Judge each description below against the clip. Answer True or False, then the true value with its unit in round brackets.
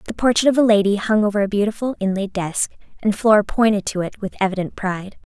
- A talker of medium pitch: False (205 Hz)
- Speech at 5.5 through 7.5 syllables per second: True (6.4 syllables/s)